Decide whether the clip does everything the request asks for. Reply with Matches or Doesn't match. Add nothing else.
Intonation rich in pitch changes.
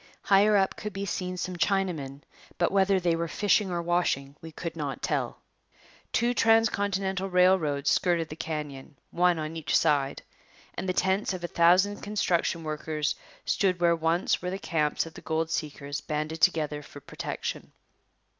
Doesn't match